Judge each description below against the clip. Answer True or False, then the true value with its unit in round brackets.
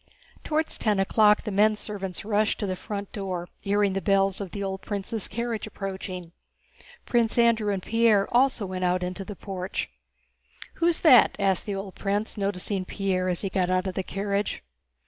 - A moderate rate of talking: True (180 wpm)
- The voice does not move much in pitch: True (2.0 semitones)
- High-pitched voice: True (200 Hz)